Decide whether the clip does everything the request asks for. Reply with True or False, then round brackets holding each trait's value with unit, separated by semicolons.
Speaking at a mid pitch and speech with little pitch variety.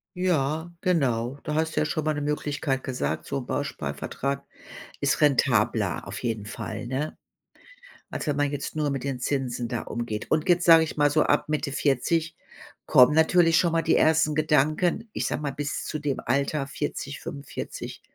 False (145 Hz; 3.1 semitones)